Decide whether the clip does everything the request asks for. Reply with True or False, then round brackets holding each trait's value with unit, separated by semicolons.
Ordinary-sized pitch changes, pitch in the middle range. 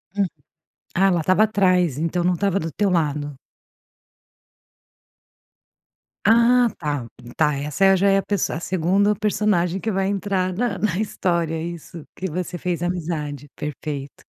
True (3.7 semitones; 180 Hz)